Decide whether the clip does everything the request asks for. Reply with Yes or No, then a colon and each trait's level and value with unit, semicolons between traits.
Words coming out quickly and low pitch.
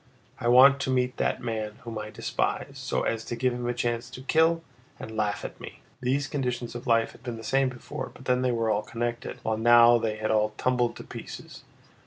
Yes: fast, 225 wpm; low, 120 Hz